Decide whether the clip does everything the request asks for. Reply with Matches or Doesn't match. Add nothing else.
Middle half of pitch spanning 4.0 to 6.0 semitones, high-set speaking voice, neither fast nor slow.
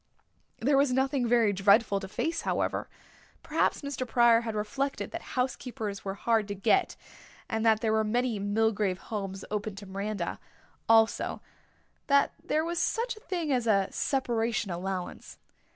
Matches